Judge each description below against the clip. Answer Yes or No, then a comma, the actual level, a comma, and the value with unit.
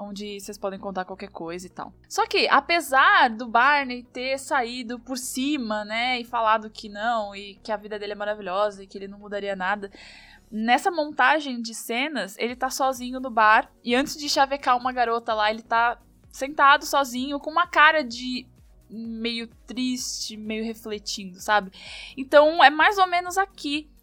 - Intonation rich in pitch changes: No, average, 4.7 semitones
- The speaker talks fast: No, average, 175 wpm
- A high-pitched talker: Yes, high, 240 Hz